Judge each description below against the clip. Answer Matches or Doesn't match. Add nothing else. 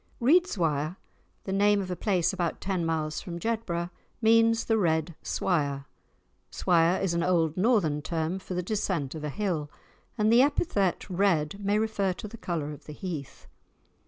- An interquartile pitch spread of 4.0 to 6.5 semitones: Matches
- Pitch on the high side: Doesn't match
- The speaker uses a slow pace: Doesn't match